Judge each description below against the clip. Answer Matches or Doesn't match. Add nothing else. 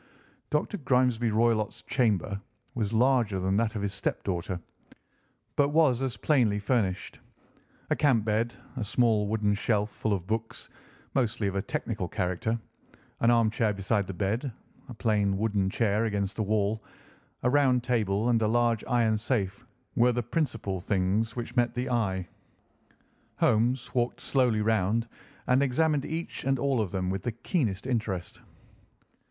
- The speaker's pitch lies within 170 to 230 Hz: Doesn't match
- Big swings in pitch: Doesn't match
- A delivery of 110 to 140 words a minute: Doesn't match